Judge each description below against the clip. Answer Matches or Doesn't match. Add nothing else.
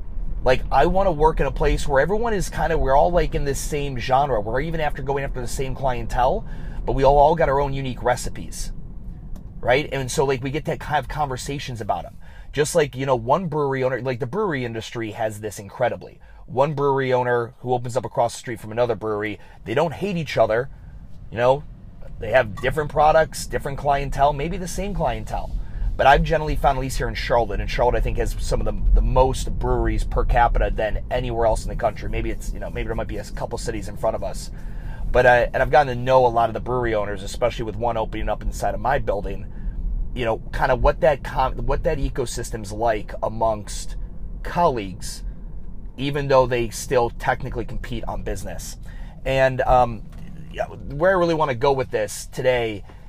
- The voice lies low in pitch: Matches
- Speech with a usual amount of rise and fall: Matches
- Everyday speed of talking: Doesn't match